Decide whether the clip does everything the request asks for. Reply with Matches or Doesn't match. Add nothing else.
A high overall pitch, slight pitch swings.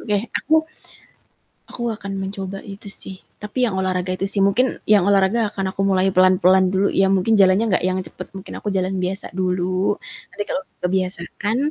Matches